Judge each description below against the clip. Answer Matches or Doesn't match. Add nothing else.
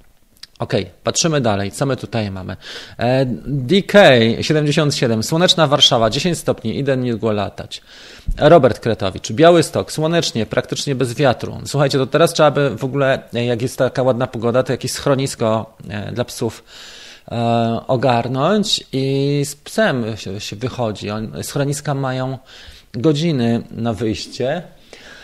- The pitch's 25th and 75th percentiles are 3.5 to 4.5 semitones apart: Matches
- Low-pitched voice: Matches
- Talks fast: Doesn't match